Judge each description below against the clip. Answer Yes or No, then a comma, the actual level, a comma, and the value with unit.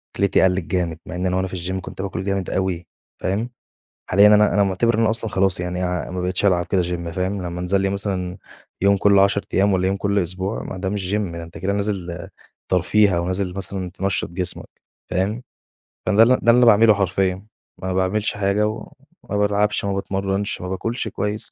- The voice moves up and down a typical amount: No, narrow, 2.0 semitones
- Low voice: Yes, very low, 95 Hz